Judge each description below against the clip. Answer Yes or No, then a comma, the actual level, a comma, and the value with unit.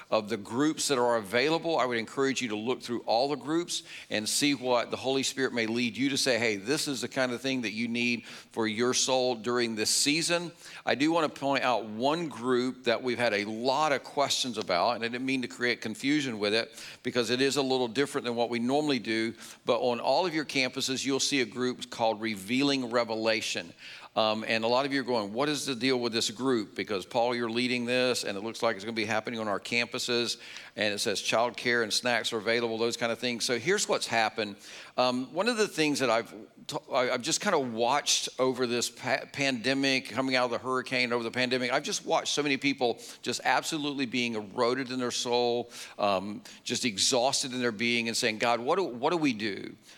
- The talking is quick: Yes, fast, 235 wpm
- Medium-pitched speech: No, low, 125 Hz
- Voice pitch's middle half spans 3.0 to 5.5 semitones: No, narrow, 2.4 semitones